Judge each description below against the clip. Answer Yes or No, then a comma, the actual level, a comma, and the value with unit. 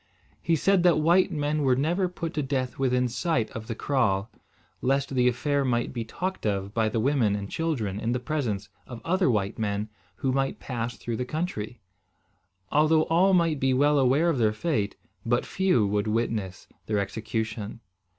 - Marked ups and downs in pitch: Yes, wide, 5.7 semitones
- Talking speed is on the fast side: No, average, 180 wpm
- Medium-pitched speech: No, low, 125 Hz